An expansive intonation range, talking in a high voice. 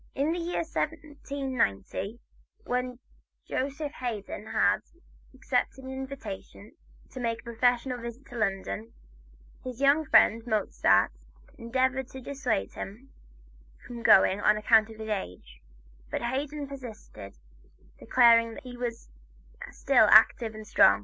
No: average, 3.6 semitones; high, 240 Hz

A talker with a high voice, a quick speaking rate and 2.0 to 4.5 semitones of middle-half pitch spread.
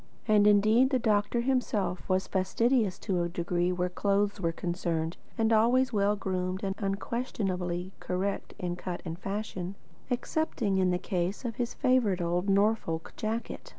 No: high, 195 Hz; average, 150 wpm; average, 3.6 semitones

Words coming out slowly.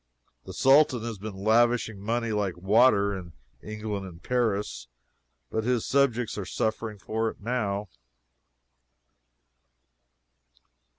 Yes: slow, 110 wpm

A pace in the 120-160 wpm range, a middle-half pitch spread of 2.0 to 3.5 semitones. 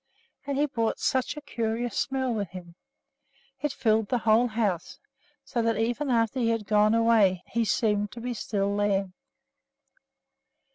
Yes: average, 155 wpm; average, 2.8 semitones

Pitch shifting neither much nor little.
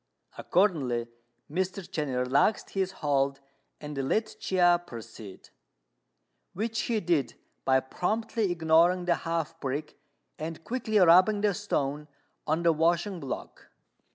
Yes: average, 4.9 semitones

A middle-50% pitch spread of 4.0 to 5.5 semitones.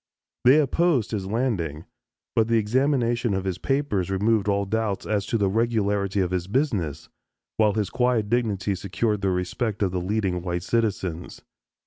No: average, 3.6 semitones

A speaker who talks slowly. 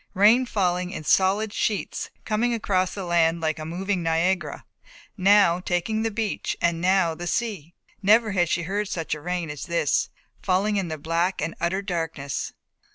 No: average, 165 wpm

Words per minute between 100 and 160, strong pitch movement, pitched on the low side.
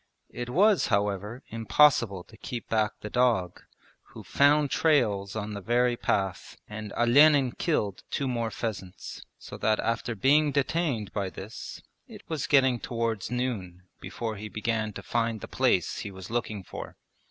No: average, 155 wpm; average, 3.7 semitones; low, 115 Hz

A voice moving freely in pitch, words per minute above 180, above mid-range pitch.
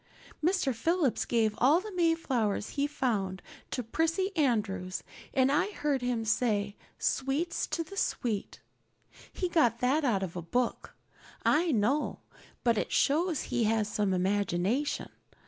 No: wide, 6.7 semitones; average, 145 wpm; very high, 250 Hz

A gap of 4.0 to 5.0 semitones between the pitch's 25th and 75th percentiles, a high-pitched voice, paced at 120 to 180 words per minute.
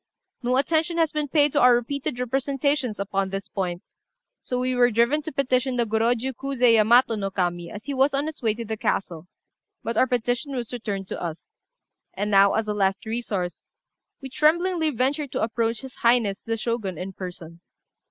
No: average, 4.7 semitones; high, 235 Hz; average, 190 wpm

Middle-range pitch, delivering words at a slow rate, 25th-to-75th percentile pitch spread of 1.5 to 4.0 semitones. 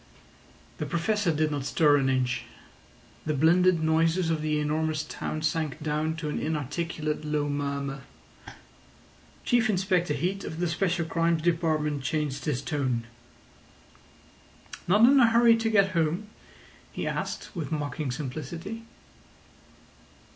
Yes: medium, 160 Hz; slow, 130 wpm; average, 2.9 semitones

